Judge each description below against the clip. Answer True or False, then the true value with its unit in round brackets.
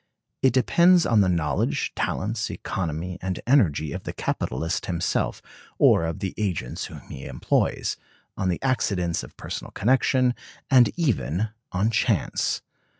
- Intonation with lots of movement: True (6.6 semitones)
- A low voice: True (95 Hz)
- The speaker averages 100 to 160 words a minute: True (140 wpm)